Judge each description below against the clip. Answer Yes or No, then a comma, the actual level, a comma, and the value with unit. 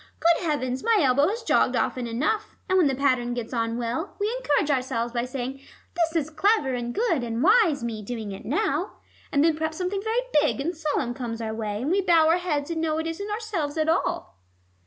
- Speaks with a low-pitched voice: No, very high, 295 Hz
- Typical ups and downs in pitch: No, wide, 6.1 semitones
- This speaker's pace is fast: Yes, fast, 220 wpm